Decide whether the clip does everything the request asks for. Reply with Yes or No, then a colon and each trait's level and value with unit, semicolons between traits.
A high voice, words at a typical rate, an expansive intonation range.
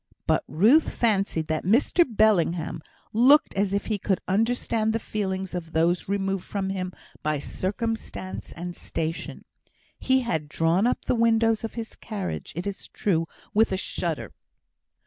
No: high, 195 Hz; average, 150 wpm; average, 4.3 semitones